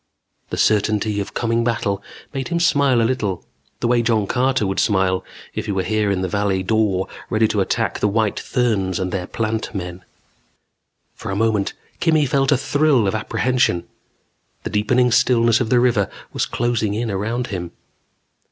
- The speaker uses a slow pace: No, average, 175 wpm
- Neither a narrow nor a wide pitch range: Yes, average, 3.7 semitones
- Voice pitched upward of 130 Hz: No, low, 110 Hz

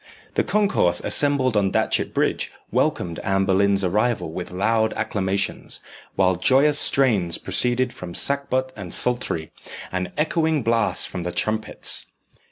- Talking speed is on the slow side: Yes, slow, 130 wpm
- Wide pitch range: Yes, wide, 5.8 semitones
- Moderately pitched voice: No, low, 110 Hz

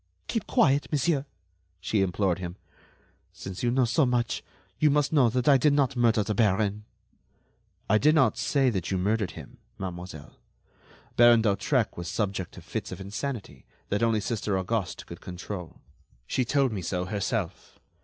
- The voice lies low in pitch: Yes, low, 110 Hz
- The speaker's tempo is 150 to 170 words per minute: Yes, average, 165 wpm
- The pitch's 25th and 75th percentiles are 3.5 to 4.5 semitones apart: No, average, 5.2 semitones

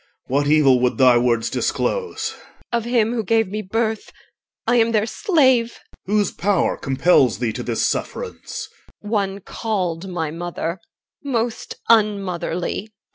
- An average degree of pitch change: No, wide, 6.2 semitones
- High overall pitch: Yes, high, 200 Hz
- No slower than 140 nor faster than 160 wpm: Yes, average, 145 wpm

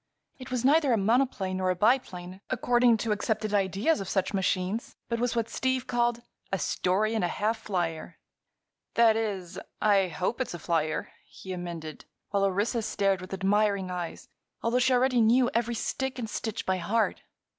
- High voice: Yes, high, 210 Hz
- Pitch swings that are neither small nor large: Yes, average, 4.2 semitones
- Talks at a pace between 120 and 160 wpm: No, average, 175 wpm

